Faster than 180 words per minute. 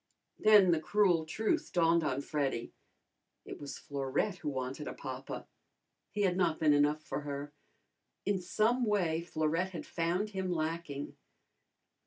No: average, 145 wpm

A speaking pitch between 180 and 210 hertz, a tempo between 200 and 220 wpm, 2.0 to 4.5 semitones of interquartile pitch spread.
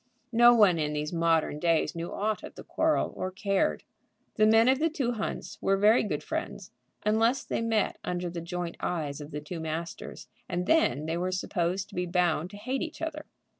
No: medium, 185 Hz; fast, 205 wpm; average, 5.1 semitones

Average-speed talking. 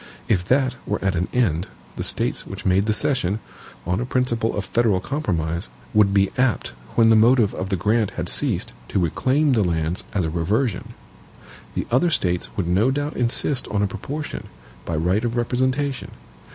Yes: average, 180 wpm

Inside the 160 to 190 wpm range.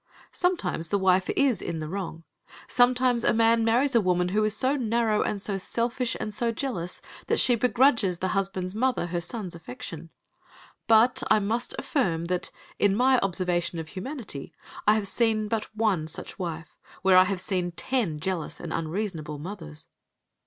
Yes: average, 170 wpm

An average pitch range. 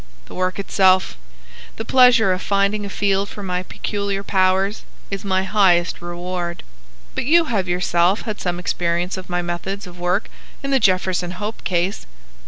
No: narrow, 2.2 semitones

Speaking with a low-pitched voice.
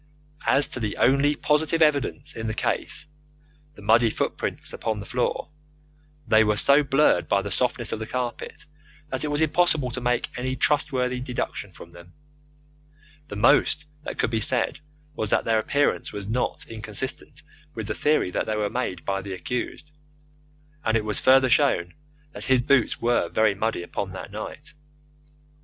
Yes: low, 120 Hz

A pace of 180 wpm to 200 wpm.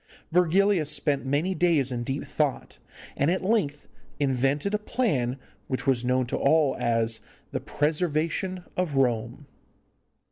No: slow, 135 wpm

